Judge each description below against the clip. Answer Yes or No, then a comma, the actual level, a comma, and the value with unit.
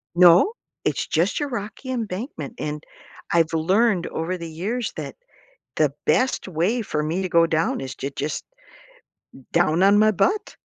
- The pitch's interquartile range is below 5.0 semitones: No, average, 5.3 semitones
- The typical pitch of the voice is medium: Yes, medium, 180 Hz